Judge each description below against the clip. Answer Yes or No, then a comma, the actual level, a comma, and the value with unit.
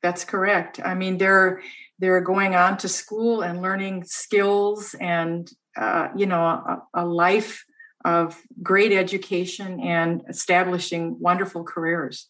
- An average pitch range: No, narrow, 2.0 semitones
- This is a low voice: No, medium, 185 Hz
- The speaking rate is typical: No, slow, 130 wpm